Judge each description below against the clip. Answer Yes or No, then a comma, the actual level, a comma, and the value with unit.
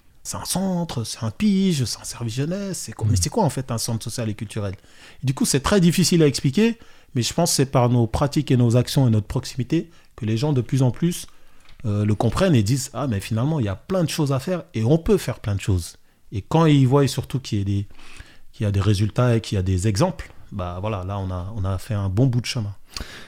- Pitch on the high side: No, low, 120 Hz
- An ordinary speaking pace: No, fast, 275 wpm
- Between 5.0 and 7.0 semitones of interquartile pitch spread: Yes, wide, 5.5 semitones